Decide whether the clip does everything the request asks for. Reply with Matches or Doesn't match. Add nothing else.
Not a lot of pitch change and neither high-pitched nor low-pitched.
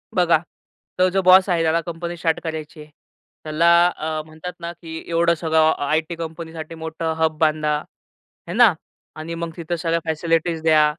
Matches